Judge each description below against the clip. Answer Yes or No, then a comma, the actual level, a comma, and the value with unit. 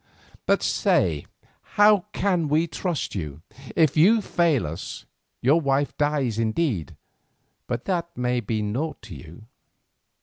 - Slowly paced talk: Yes, slow, 130 wpm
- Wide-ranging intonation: Yes, wide, 7.5 semitones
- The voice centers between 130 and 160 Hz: Yes, medium, 140 Hz